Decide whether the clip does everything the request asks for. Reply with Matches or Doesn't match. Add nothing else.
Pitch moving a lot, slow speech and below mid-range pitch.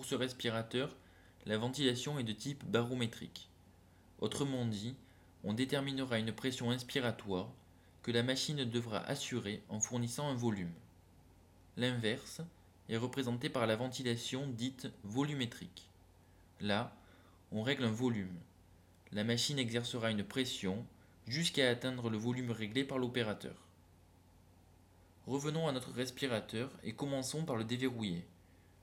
Matches